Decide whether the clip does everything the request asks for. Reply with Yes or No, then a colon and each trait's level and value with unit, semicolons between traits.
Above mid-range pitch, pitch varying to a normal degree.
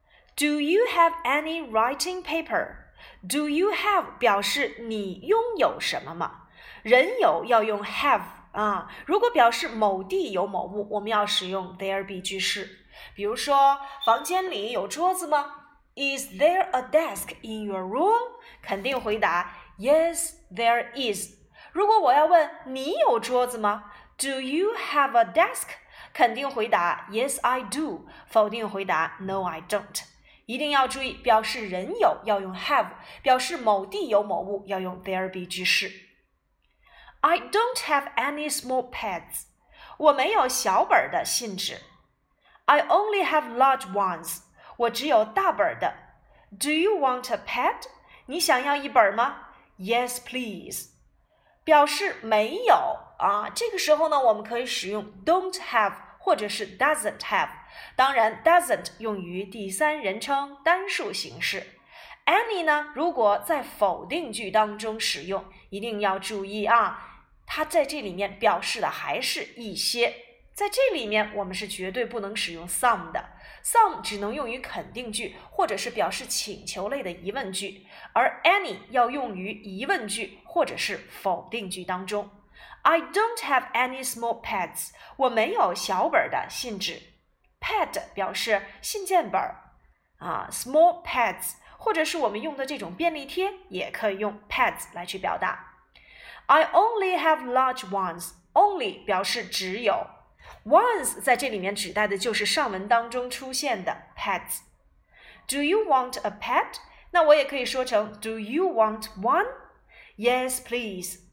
No: very high, 250 Hz; wide, 7.5 semitones